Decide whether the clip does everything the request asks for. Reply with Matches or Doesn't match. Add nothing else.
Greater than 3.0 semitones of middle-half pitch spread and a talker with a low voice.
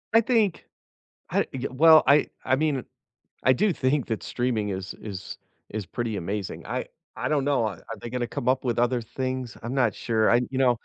Matches